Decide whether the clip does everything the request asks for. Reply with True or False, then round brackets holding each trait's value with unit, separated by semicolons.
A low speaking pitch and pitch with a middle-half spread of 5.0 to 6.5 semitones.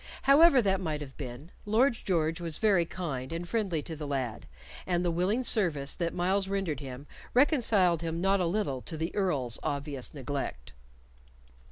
False (170 Hz; 5.4 semitones)